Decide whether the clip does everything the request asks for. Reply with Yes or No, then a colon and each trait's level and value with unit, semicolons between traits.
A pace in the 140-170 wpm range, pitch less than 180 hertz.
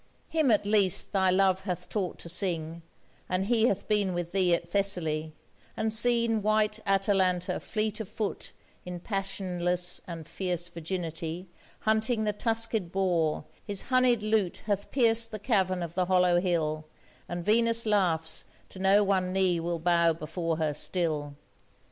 No: average, 155 wpm; medium, 185 Hz